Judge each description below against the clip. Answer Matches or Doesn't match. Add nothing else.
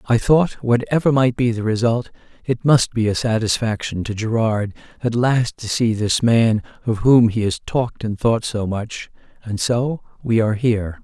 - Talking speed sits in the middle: Matches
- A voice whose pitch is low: Matches